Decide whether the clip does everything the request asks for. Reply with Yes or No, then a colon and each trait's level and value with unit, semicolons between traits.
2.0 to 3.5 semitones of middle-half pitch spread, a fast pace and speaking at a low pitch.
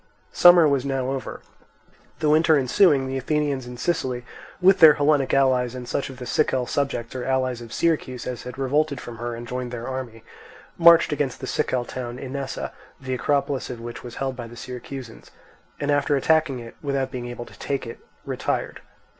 No: narrow, 2.6 semitones; average, 190 wpm; low, 130 Hz